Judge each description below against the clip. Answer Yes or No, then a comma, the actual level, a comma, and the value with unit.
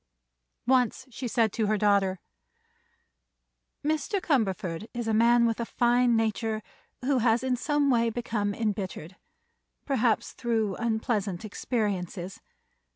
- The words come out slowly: Yes, slow, 120 wpm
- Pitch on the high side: Yes, high, 225 Hz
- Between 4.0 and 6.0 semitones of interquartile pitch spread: No, average, 2.8 semitones